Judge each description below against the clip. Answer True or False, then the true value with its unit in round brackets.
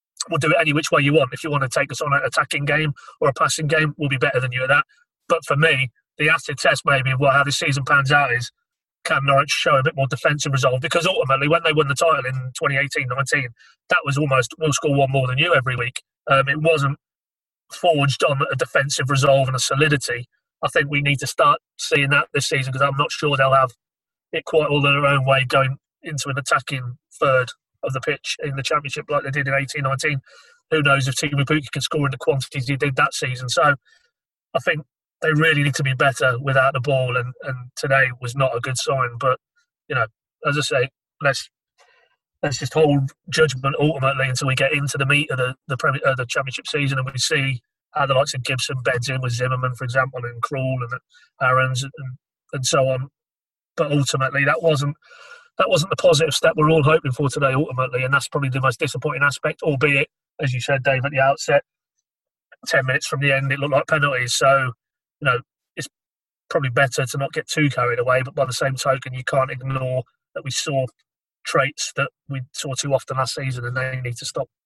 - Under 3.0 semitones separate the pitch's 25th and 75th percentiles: True (2.5 semitones)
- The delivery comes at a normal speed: False (225 wpm)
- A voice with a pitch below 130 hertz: False (140 Hz)